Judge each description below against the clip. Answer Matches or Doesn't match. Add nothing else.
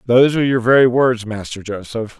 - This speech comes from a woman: Doesn't match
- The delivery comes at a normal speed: Matches